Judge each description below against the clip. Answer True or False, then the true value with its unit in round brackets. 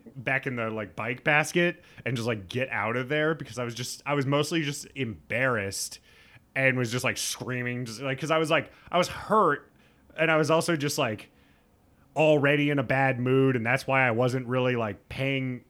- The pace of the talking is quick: True (210 wpm)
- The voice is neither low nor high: False (130 Hz)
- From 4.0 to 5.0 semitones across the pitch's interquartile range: False (3.5 semitones)